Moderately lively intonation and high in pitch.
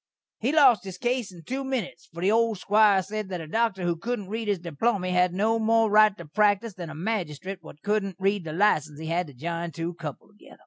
Yes: average, 4.2 semitones; high, 195 Hz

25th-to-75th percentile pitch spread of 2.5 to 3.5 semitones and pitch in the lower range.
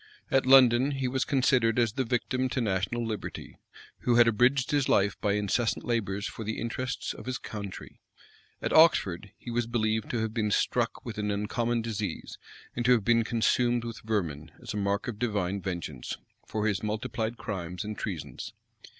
Yes: average, 3.0 semitones; low, 110 Hz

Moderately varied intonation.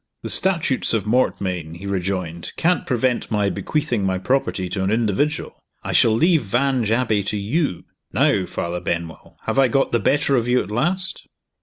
No: wide, 6.1 semitones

